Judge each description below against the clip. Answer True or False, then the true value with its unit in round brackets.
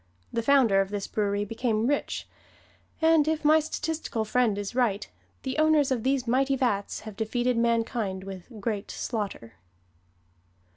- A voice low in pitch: False (230 Hz)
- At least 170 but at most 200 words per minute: False (145 wpm)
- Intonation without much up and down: False (4.7 semitones)